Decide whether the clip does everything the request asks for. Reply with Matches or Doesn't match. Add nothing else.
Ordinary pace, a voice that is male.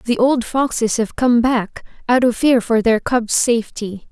Doesn't match